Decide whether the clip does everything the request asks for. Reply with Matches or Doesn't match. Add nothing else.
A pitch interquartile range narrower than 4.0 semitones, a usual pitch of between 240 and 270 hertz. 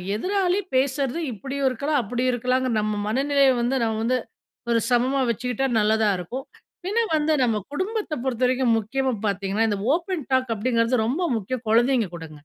Matches